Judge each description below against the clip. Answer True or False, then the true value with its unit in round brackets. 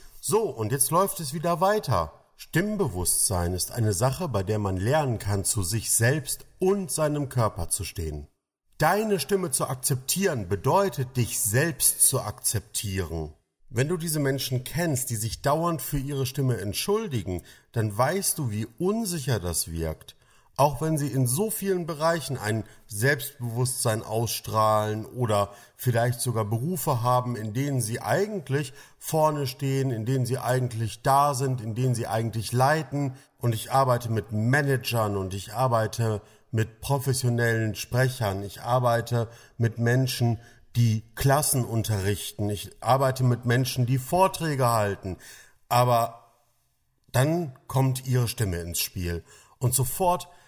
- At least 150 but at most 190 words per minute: False (140 wpm)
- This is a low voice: True (125 Hz)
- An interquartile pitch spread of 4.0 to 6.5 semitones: True (4.3 semitones)